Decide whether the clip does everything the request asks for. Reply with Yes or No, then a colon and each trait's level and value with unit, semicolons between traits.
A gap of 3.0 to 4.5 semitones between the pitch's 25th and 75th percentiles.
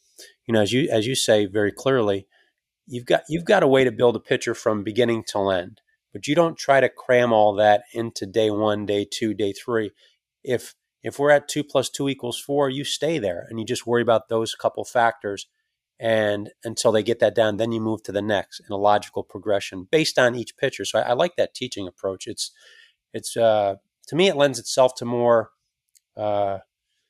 Yes: average, 4.2 semitones